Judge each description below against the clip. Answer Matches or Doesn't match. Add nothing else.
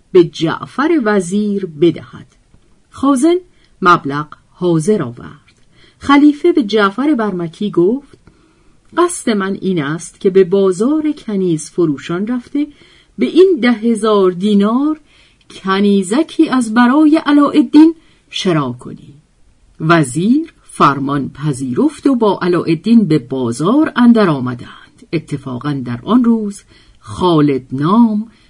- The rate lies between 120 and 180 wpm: Doesn't match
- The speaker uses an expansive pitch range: Matches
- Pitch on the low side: Doesn't match